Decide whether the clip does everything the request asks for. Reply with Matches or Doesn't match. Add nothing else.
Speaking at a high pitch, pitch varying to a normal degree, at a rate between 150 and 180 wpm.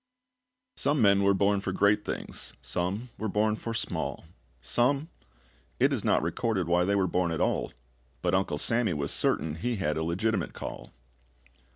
Doesn't match